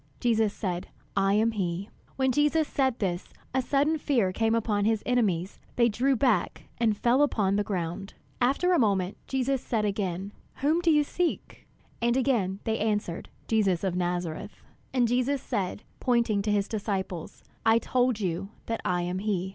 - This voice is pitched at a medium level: No, high, 220 Hz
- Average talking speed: Yes, average, 170 wpm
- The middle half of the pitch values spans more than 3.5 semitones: Yes, average, 4.5 semitones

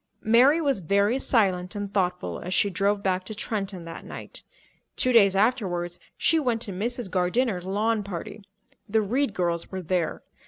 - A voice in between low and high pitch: No, high, 200 Hz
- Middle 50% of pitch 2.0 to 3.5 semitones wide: No, average, 3.9 semitones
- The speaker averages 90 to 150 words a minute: No, average, 165 wpm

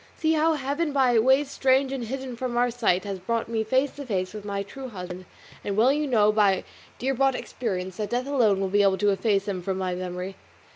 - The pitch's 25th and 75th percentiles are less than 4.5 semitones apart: No, average, 5.3 semitones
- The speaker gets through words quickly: Yes, fast, 230 wpm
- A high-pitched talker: Yes, high, 225 Hz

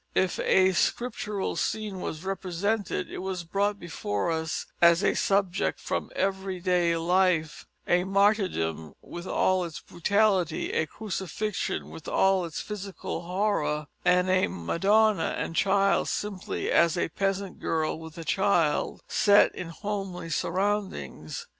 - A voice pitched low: No, medium, 185 Hz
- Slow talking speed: Yes, slow, 130 wpm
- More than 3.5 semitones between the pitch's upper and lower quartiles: No, average, 3.1 semitones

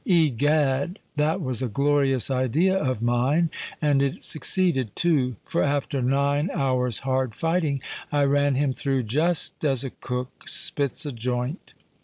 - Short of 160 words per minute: Yes, average, 140 wpm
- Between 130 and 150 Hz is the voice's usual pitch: Yes, medium, 140 Hz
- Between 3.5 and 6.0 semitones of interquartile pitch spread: No, average, 2.9 semitones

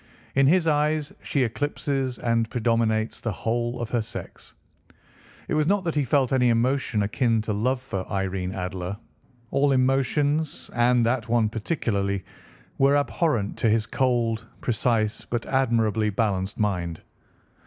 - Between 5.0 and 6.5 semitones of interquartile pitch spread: No, average, 3.9 semitones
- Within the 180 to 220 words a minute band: No, average, 145 wpm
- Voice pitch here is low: Yes, low, 120 Hz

